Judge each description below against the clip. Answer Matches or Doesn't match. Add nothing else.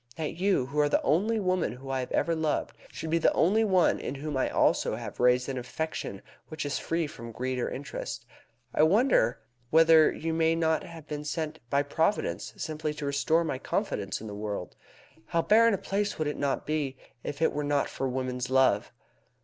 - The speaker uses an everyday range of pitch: Matches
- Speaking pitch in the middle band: Matches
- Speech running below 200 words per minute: Doesn't match